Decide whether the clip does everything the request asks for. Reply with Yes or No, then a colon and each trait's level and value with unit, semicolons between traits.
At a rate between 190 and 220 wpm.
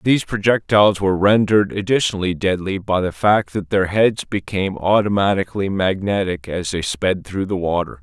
No: average, 155 wpm